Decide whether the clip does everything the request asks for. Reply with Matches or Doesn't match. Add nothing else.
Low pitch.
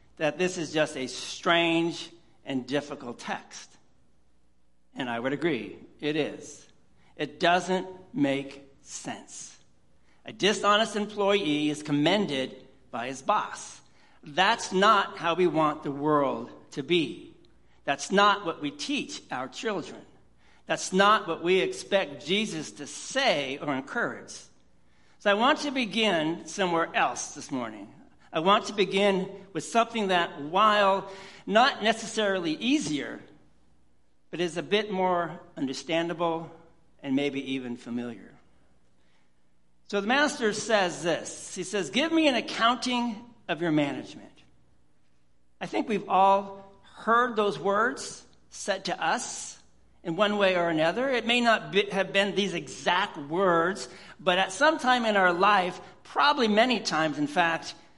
Doesn't match